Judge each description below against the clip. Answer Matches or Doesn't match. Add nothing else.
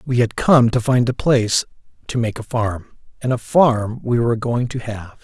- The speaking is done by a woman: Doesn't match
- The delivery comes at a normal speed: Doesn't match